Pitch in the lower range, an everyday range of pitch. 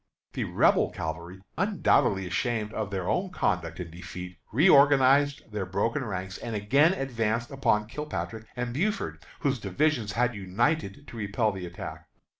No: low, 110 Hz; wide, 6.3 semitones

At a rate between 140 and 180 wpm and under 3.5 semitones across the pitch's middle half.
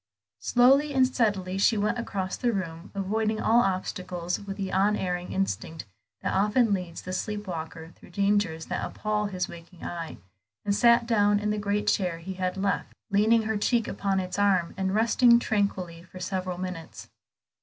Yes: average, 165 wpm; average, 2.7 semitones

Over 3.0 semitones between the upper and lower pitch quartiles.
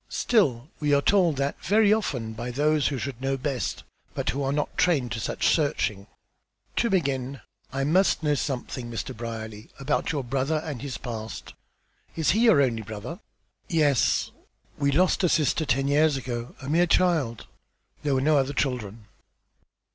Yes: average, 4.1 semitones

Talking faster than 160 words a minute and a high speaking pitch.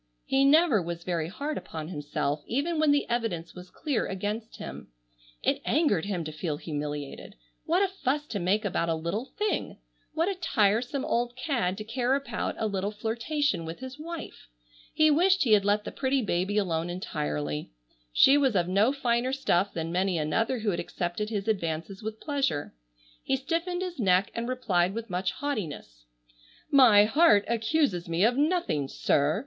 Yes: average, 175 wpm; high, 215 Hz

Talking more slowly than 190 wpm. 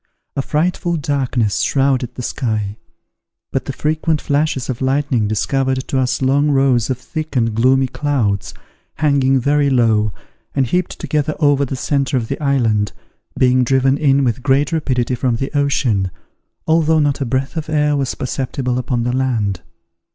Yes: average, 160 wpm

